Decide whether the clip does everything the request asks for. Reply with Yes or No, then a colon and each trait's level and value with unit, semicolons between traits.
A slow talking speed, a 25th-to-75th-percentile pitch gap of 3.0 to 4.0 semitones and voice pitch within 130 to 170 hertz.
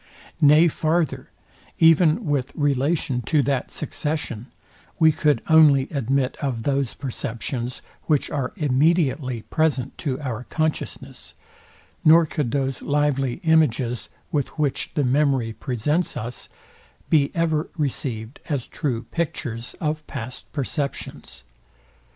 Yes: slow, 115 wpm; average, 3.4 semitones; medium, 140 Hz